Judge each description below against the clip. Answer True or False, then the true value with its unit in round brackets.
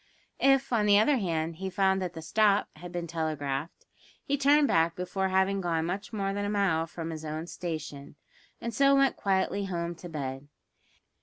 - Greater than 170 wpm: True (185 wpm)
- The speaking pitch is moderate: True (180 Hz)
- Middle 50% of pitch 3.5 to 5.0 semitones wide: True (3.9 semitones)